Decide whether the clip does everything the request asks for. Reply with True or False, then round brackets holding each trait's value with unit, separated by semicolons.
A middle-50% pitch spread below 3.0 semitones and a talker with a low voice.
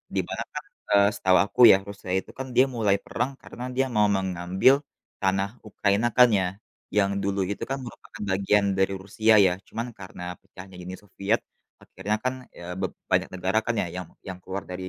True (2.5 semitones; 100 Hz)